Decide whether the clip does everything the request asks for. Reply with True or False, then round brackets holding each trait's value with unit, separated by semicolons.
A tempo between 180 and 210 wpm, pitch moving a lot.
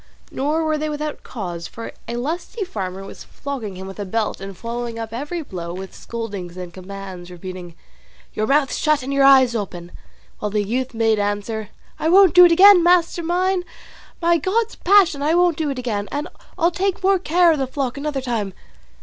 True (195 wpm; 8.3 semitones)